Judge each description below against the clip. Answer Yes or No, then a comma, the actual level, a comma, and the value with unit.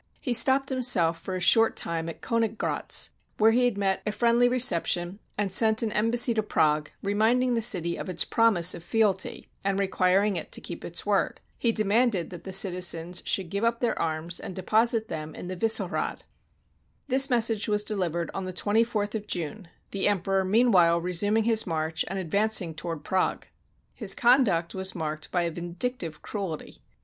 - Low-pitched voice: No, high, 195 Hz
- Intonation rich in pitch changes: No, average, 4.6 semitones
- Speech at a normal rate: Yes, average, 180 wpm